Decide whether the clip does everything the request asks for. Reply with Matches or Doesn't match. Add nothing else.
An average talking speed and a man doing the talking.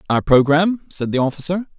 Matches